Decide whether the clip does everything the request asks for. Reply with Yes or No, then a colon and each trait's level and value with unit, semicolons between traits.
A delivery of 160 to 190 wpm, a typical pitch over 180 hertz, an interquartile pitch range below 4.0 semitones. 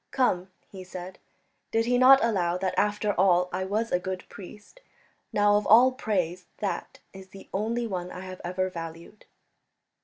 Yes: average, 165 wpm; high, 190 Hz; average, 2.8 semitones